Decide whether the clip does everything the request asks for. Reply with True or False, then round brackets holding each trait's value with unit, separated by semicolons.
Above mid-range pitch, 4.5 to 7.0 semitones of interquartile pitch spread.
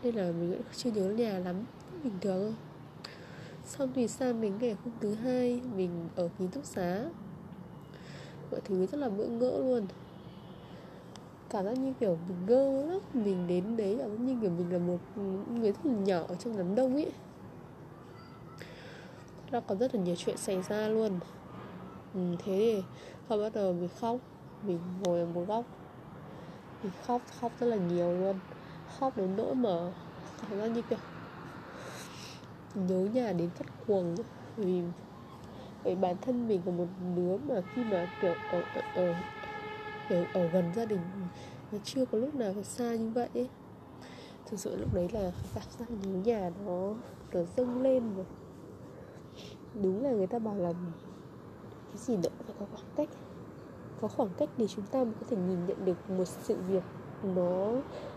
True (200 Hz; 4.9 semitones)